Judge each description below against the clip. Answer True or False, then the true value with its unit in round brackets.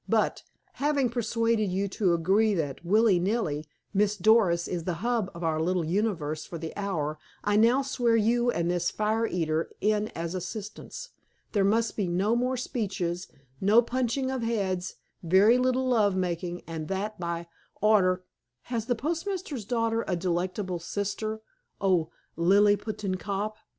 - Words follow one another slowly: False (150 wpm)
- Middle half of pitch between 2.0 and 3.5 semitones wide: False (4.4 semitones)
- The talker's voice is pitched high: True (205 Hz)